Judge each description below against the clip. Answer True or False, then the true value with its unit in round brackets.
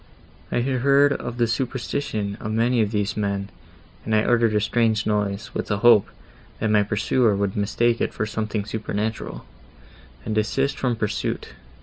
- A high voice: False (110 Hz)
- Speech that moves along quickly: False (165 wpm)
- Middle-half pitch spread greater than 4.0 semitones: False (2.4 semitones)